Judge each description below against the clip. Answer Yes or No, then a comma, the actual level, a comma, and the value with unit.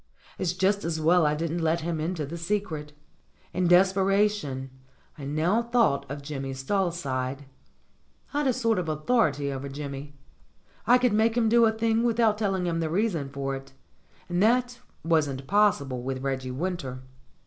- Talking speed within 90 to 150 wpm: No, average, 165 wpm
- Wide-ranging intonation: Yes, wide, 6.9 semitones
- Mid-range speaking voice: Yes, medium, 170 Hz